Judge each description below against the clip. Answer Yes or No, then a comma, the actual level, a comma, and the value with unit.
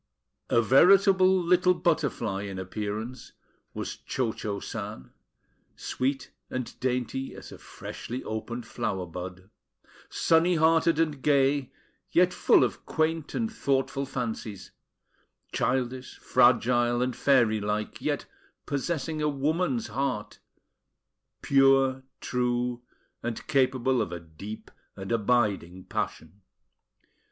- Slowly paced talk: Yes, slow, 110 wpm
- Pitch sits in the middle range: No, low, 125 Hz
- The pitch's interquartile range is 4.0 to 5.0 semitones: Yes, average, 4.6 semitones